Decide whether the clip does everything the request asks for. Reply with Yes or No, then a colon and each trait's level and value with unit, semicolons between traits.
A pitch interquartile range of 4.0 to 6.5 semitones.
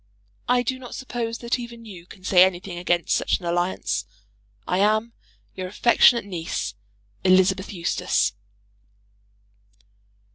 Yes: average, 4.6 semitones